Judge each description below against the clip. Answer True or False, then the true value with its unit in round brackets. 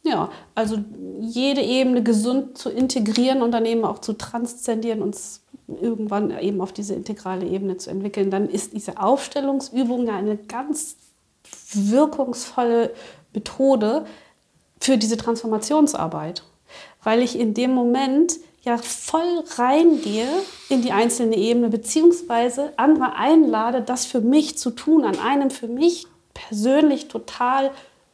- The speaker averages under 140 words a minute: True (130 wpm)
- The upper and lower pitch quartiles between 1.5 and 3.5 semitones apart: False (3.9 semitones)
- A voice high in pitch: True (245 Hz)